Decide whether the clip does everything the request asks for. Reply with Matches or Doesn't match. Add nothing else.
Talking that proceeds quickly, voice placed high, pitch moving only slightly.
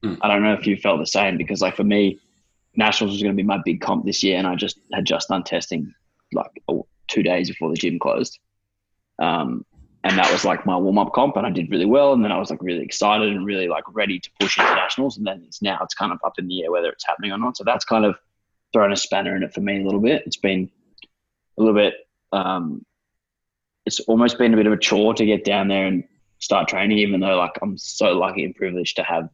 Doesn't match